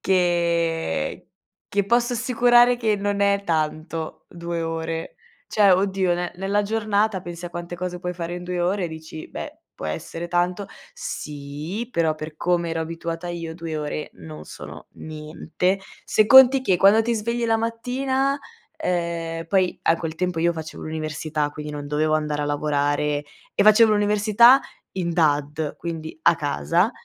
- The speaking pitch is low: No, medium, 170 Hz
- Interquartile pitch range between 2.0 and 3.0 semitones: No, average, 4.3 semitones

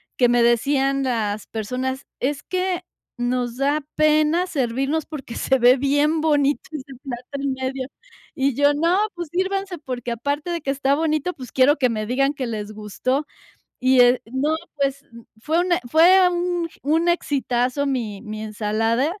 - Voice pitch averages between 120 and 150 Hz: No, very high, 275 Hz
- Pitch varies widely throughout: No, average, 3.9 semitones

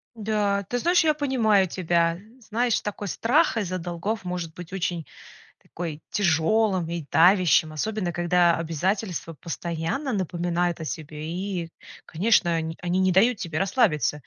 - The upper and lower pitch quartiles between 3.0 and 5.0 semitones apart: Yes, average, 4.1 semitones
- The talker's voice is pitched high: No, medium, 180 Hz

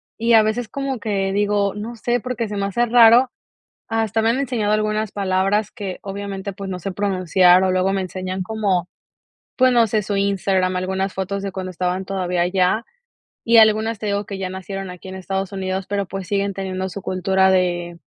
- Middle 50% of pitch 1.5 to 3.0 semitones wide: Yes, narrow, 2.4 semitones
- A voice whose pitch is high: Yes, high, 195 Hz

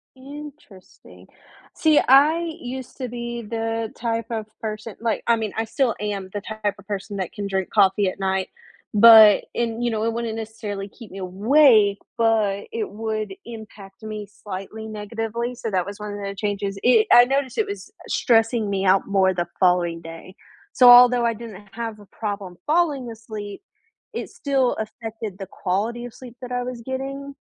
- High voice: Yes, high, 220 Hz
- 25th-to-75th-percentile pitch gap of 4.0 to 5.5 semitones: No, average, 3.1 semitones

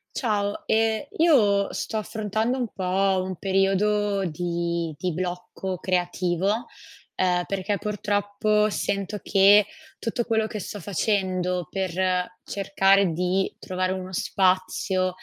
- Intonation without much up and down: Yes, narrow, 2.2 semitones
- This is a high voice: Yes, high, 195 Hz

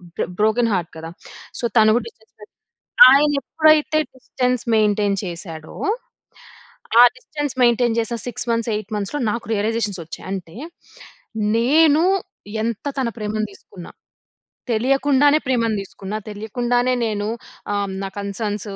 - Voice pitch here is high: Yes, high, 225 Hz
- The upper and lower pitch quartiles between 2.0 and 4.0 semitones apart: Yes, average, 3.5 semitones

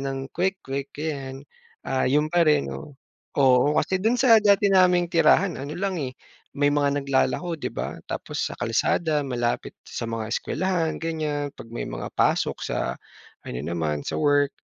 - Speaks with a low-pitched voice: No, medium, 145 Hz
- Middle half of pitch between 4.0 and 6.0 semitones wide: Yes, average, 4.7 semitones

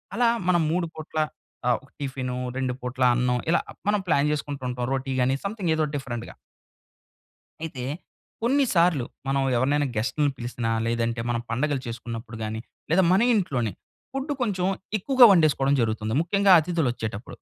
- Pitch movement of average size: No, wide, 6.1 semitones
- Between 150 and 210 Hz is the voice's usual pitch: No, medium, 140 Hz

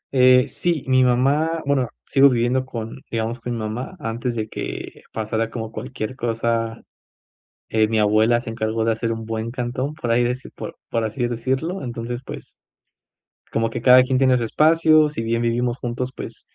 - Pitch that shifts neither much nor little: No, narrow, 2.3 semitones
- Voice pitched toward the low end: Yes, low, 120 Hz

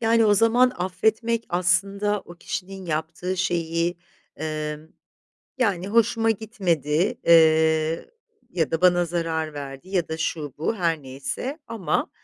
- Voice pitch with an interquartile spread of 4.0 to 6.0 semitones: Yes, average, 4.4 semitones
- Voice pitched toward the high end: No, medium, 175 Hz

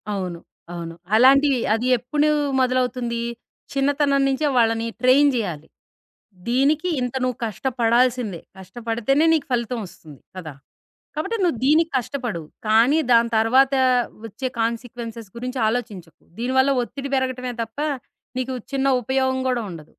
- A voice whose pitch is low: No, high, 245 Hz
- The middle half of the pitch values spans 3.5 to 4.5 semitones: No, average, 3.1 semitones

